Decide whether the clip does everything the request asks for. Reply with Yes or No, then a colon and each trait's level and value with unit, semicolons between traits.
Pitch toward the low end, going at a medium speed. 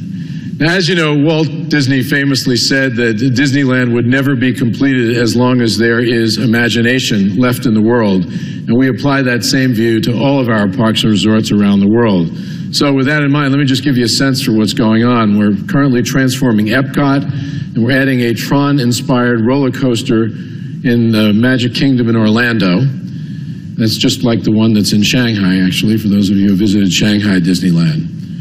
Yes: low, 125 Hz; average, 190 wpm